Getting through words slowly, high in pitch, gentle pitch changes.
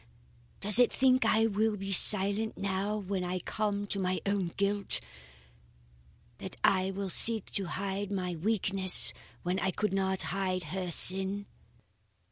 No: average, 145 wpm; high, 195 Hz; narrow, 1.5 semitones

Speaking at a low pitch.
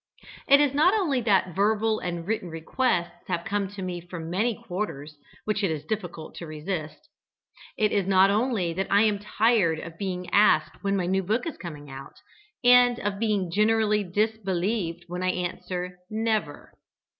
No: high, 195 Hz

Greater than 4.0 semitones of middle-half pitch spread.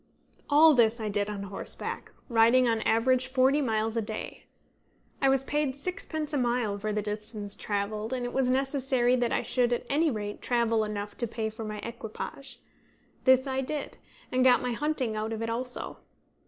No: average, 3.4 semitones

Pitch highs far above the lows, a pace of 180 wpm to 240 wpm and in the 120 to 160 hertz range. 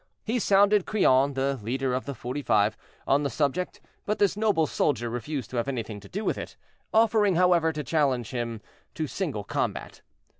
Yes: wide, 7.0 semitones; average, 185 wpm; medium, 140 Hz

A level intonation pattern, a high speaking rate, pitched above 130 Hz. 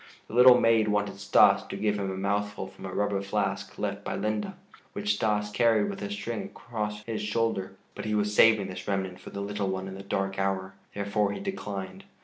No: narrow, 1.6 semitones; fast, 210 wpm; low, 105 Hz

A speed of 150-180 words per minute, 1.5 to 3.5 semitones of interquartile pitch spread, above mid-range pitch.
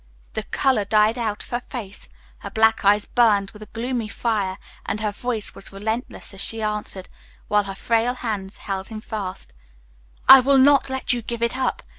No: average, 190 wpm; average, 2.9 semitones; high, 220 Hz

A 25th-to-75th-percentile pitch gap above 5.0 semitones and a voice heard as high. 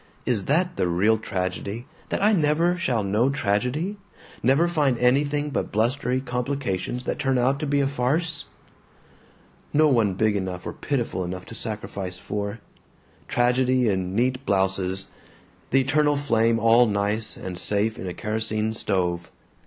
No: wide, 5.5 semitones; low, 120 Hz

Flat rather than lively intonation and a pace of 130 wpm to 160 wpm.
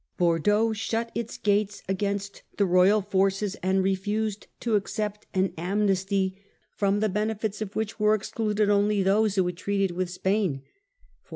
Yes: narrow, 1.8 semitones; average, 155 wpm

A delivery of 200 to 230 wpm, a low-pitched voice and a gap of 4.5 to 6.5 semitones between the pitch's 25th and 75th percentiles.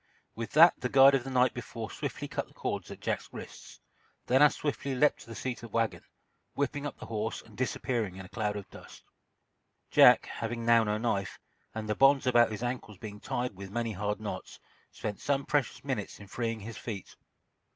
No: fast, 205 wpm; low, 115 Hz; average, 3.5 semitones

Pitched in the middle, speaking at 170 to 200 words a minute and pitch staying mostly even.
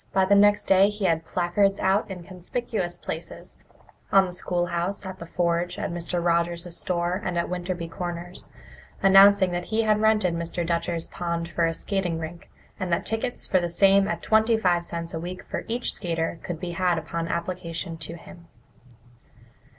Yes: medium, 175 Hz; average, 180 wpm; narrow, 2.3 semitones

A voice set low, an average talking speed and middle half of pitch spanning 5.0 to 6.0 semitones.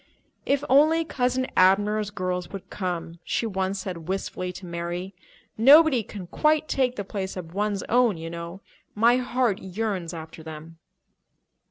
No: high, 195 Hz; average, 150 wpm; wide, 5.5 semitones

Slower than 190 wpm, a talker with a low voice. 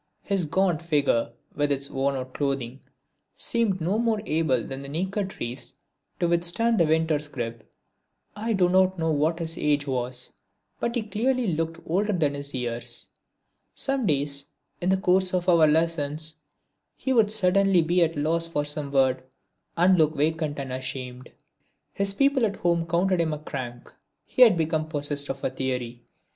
No: average, 170 wpm; medium, 160 Hz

